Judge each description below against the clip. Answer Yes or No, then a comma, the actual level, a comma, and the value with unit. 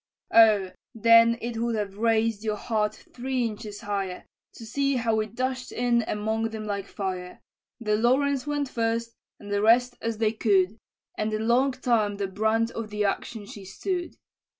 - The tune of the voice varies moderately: No, narrow, 2.2 semitones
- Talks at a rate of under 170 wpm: No, average, 175 wpm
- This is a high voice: Yes, high, 225 Hz